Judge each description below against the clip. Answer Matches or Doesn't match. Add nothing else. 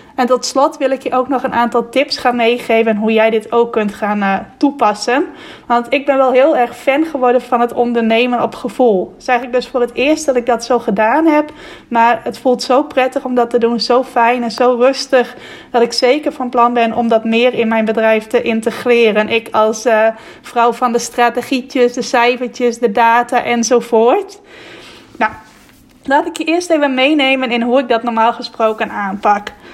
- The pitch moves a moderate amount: Doesn't match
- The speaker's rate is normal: Doesn't match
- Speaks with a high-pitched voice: Matches